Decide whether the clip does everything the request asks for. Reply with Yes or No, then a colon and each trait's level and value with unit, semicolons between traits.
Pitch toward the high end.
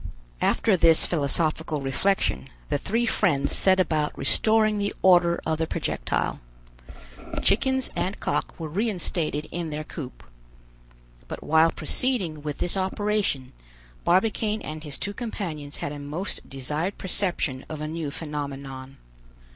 No: medium, 165 Hz